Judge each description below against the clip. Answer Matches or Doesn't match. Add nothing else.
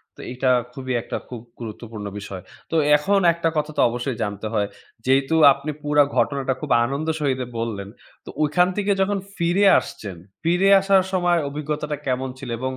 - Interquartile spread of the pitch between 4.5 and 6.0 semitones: Matches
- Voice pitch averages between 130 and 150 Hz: Matches